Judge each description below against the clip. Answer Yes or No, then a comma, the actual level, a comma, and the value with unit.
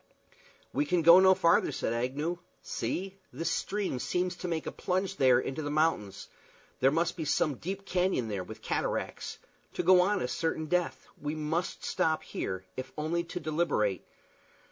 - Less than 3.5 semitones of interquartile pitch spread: No, average, 5.0 semitones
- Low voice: No, medium, 160 Hz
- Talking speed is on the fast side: No, average, 170 wpm